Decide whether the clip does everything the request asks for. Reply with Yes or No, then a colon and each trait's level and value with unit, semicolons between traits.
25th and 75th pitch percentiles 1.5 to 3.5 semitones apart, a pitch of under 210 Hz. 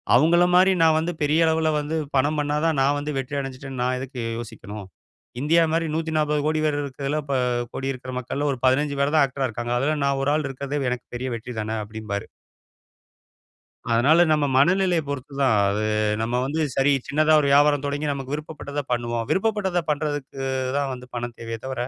Yes: average, 3.1 semitones; medium, 140 Hz